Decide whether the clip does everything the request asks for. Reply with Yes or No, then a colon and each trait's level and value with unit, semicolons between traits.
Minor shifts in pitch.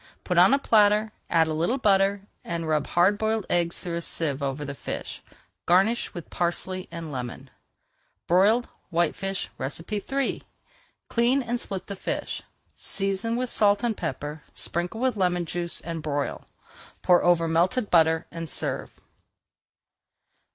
No: average, 4.2 semitones